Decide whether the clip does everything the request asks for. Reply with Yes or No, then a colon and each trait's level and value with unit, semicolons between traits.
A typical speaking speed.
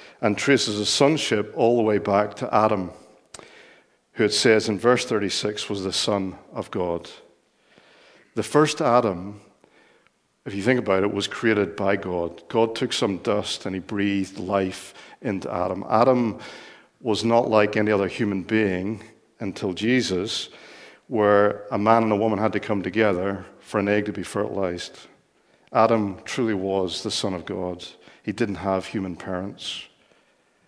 Yes: average, 160 wpm